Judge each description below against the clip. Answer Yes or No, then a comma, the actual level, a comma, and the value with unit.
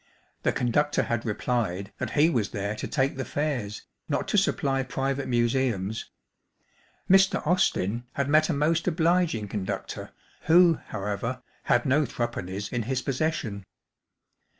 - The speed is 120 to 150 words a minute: Yes, average, 140 wpm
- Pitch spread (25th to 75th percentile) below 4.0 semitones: No, wide, 5.5 semitones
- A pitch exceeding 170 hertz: No, low, 130 Hz